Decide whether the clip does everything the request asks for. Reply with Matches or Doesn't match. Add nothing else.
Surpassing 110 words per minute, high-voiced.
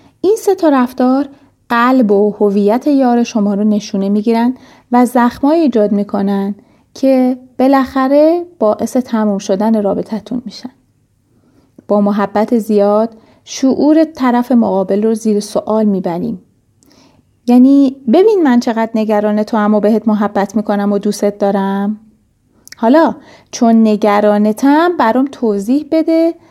Matches